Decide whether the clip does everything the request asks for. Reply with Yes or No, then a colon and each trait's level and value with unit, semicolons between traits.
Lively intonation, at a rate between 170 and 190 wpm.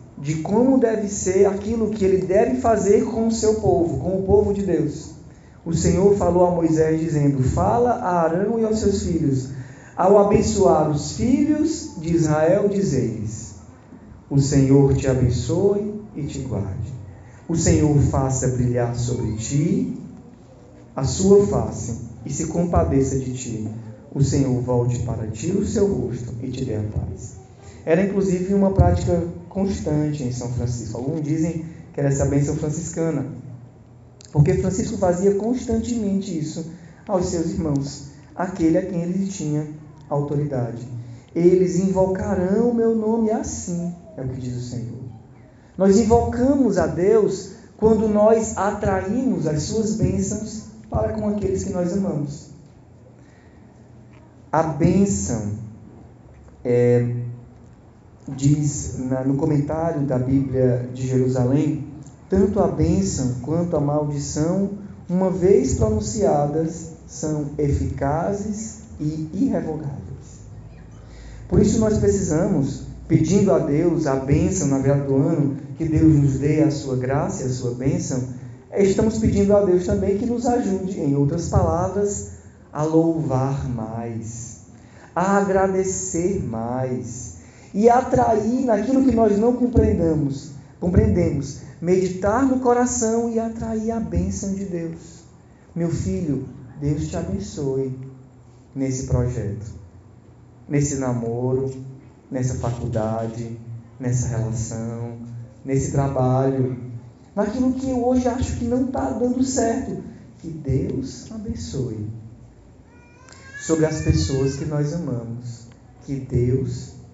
No: wide, 7.3 semitones; average, 125 wpm